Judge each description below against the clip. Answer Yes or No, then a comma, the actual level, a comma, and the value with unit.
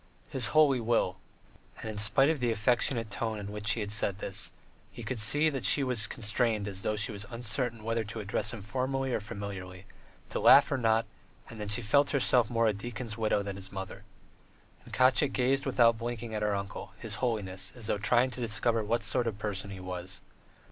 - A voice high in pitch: No, low, 110 Hz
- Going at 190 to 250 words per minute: Yes, fast, 205 wpm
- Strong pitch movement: No, average, 3.1 semitones